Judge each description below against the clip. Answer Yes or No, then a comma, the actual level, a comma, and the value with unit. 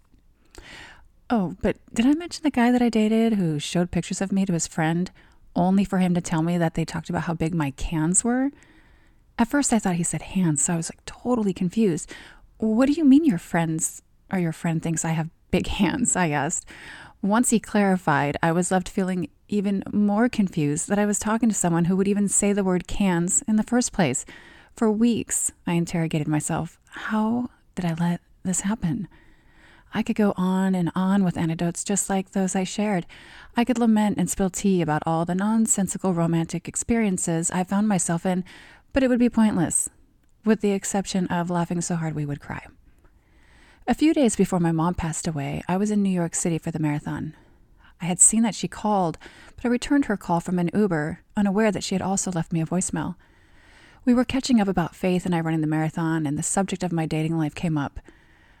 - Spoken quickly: Yes, fast, 210 wpm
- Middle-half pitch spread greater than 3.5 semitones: Yes, average, 4.3 semitones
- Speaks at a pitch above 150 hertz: Yes, medium, 185 Hz